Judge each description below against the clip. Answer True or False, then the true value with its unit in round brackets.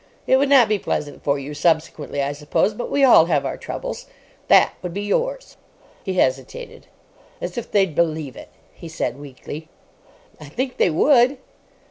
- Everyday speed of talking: True (170 wpm)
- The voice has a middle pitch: True (170 Hz)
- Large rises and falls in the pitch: True (8.4 semitones)